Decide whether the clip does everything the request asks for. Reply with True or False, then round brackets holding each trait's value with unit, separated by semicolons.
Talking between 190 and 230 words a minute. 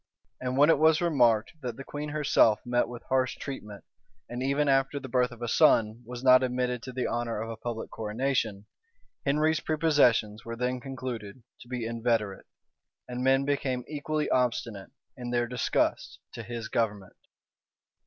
False (165 wpm)